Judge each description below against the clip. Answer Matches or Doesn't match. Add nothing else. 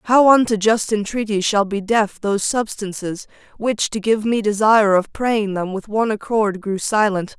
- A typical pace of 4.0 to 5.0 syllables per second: Matches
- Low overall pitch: Doesn't match